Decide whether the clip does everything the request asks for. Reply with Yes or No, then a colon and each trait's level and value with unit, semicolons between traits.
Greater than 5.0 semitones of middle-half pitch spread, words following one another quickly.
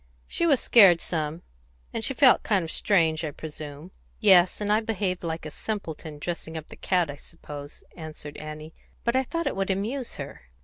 No: wide, 5.4 semitones; average, 190 wpm